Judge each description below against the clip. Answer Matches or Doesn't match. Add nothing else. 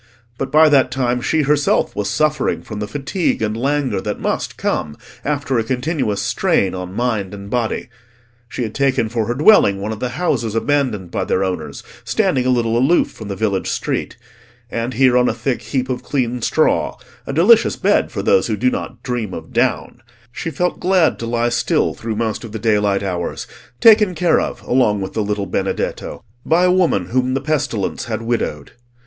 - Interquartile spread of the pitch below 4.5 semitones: Doesn't match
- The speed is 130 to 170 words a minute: Doesn't match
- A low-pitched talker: Matches